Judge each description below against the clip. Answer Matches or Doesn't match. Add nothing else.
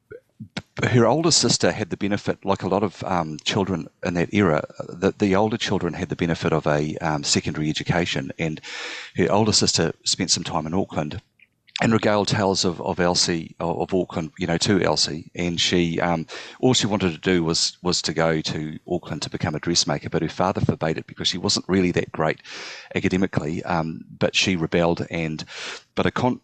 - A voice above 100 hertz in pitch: Doesn't match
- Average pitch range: Matches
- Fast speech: Doesn't match